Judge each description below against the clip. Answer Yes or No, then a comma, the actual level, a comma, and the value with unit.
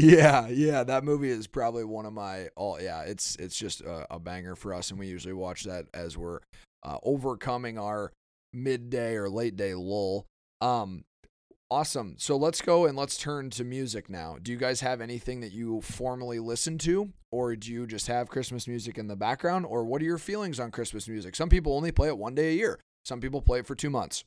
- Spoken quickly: Yes, fast, 225 wpm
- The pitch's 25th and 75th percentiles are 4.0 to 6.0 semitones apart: Yes, average, 4.6 semitones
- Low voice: Yes, low, 120 Hz